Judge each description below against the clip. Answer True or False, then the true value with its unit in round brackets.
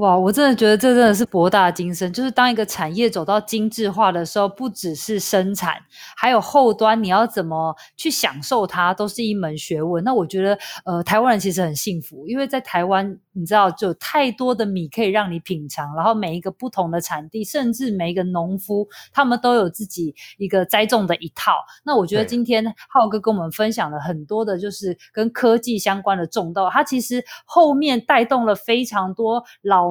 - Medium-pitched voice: False (210 Hz)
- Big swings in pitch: False (4.3 semitones)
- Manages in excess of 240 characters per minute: True (305 characters per minute)